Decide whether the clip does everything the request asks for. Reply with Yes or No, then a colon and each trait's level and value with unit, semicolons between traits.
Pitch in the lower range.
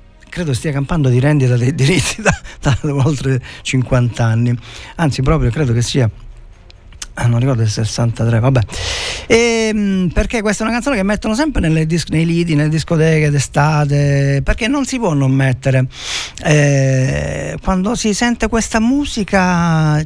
No: medium, 145 Hz